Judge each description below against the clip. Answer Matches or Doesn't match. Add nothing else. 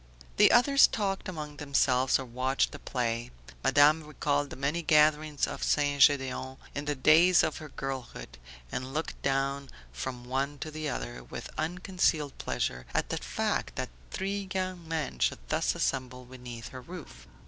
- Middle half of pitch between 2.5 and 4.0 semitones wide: Matches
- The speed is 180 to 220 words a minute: Doesn't match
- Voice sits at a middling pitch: Matches